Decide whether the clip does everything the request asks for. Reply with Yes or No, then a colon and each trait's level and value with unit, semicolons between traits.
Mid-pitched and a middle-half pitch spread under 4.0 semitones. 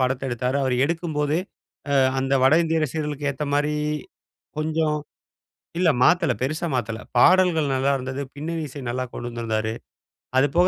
Yes: medium, 145 Hz; average, 3.6 semitones